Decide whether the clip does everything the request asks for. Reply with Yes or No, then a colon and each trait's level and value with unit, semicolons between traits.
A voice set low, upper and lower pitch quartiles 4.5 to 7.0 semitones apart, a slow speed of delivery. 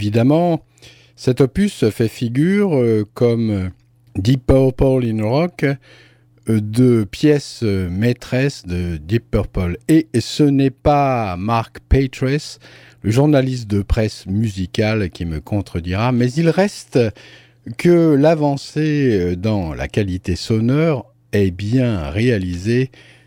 Yes: low, 120 Hz; average, 5.1 semitones; slow, 110 wpm